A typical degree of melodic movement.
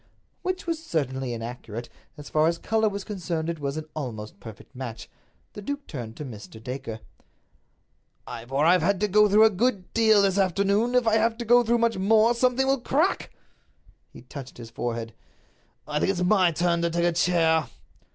No: wide, 8.6 semitones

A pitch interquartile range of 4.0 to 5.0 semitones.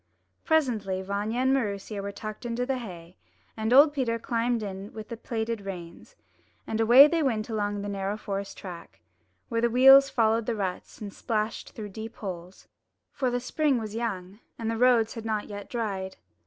No: average, 3.1 semitones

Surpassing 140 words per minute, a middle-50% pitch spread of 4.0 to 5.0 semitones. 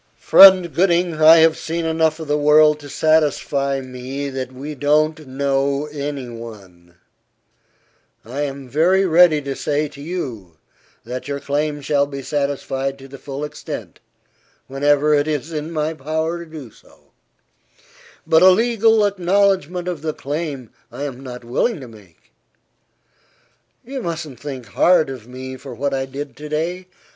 No: average, 155 wpm; average, 3.1 semitones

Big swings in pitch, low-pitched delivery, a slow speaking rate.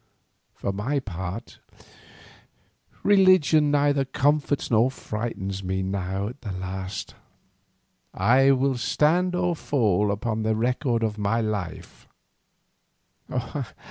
Yes: wide, 6.2 semitones; low, 115 Hz; slow, 105 wpm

